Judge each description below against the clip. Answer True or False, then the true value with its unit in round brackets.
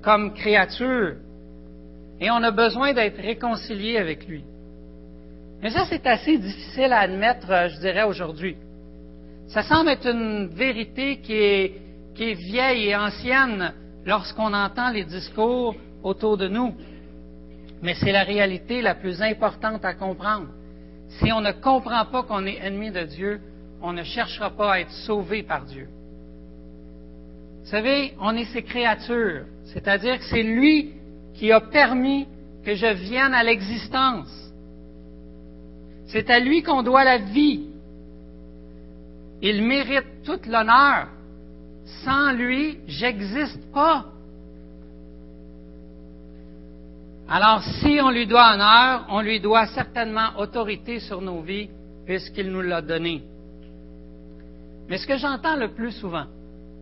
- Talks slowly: True (130 wpm)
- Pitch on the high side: True (200 Hz)